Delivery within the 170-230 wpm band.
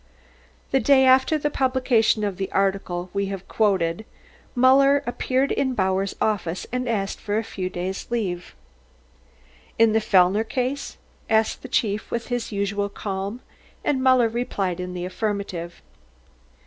No: average, 145 wpm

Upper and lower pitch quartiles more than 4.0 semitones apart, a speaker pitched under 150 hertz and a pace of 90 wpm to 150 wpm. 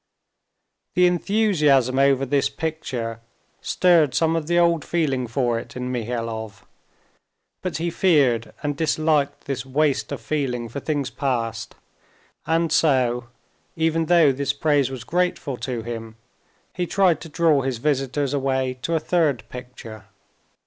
Yes: average, 4.6 semitones; medium, 140 Hz; average, 140 wpm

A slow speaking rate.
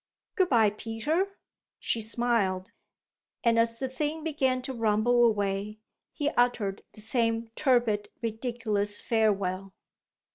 Yes: slow, 115 wpm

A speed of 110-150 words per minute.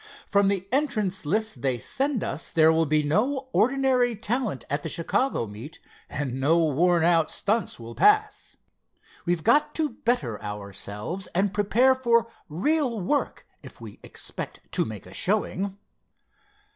Yes: average, 145 wpm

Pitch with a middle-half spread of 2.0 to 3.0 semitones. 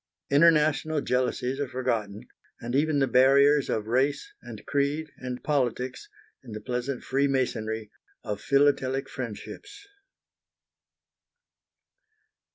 Yes: average, 2.7 semitones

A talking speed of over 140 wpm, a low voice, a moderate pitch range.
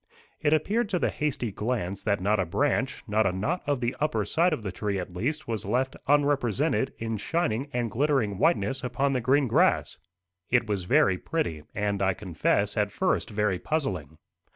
No: average, 185 wpm; low, 120 Hz; wide, 6.2 semitones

